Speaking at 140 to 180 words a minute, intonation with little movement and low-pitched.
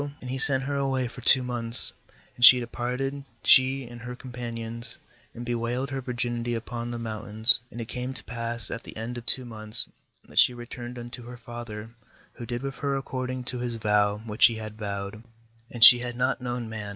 No: fast, 205 wpm; narrow, 1.6 semitones; low, 120 Hz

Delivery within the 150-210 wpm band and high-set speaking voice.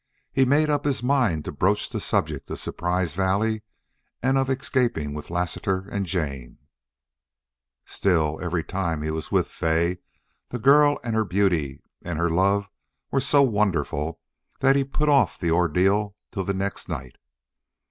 No: average, 160 wpm; very low, 95 Hz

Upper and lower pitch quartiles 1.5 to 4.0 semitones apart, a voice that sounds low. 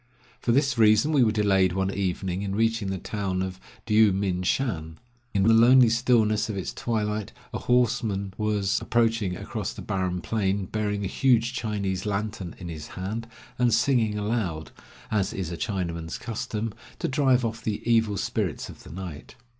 Yes: average, 3.1 semitones; low, 105 Hz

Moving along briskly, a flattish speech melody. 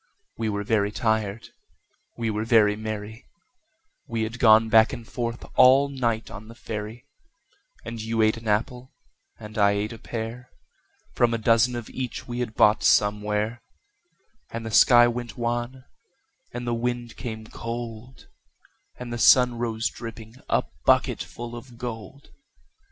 No: average, 150 wpm; narrow, 1.7 semitones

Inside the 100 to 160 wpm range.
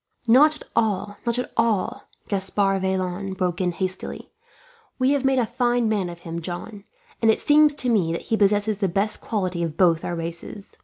No: average, 195 wpm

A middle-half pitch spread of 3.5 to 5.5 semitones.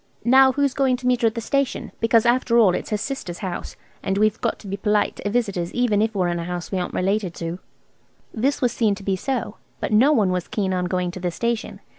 Yes: average, 4.7 semitones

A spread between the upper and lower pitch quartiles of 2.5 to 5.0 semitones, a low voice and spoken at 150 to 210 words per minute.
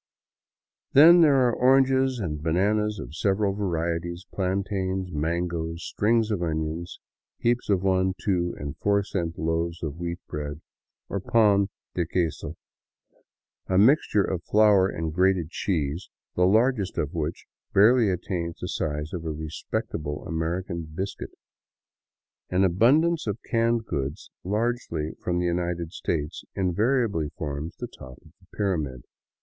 No: average, 4.2 semitones; very low, 90 Hz; average, 140 wpm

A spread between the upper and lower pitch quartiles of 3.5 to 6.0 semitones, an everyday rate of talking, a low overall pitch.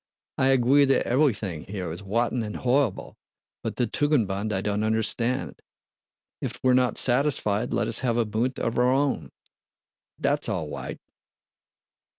Yes: average, 3.8 semitones; average, 150 wpm; low, 120 Hz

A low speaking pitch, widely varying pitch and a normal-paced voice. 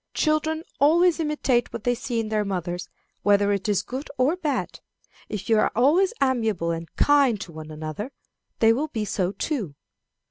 No: high, 225 Hz; wide, 6.5 semitones; average, 175 wpm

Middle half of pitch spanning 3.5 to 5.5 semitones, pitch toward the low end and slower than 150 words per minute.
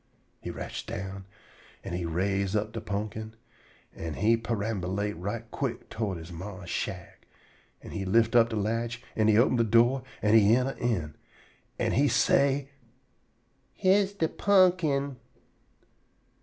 Yes: average, 3.8 semitones; low, 110 Hz; average, 140 wpm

